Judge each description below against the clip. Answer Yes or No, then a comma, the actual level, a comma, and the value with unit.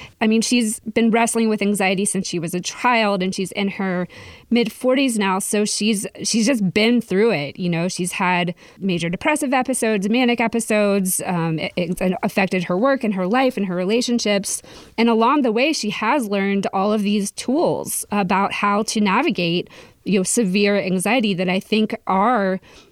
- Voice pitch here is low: No, high, 205 Hz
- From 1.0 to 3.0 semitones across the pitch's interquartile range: No, average, 3.5 semitones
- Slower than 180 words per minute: No, average, 185 wpm